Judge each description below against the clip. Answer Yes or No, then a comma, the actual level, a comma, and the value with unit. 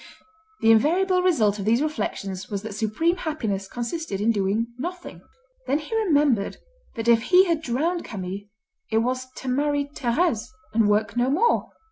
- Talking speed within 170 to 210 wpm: No, average, 160 wpm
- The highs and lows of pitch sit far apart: Yes, wide, 6.7 semitones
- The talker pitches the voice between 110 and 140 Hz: No, high, 245 Hz